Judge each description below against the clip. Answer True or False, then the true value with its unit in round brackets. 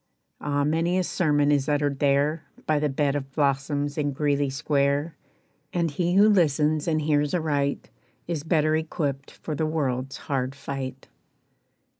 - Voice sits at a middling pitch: True (145 Hz)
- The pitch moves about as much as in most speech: False (1.9 semitones)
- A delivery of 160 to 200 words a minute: False (150 wpm)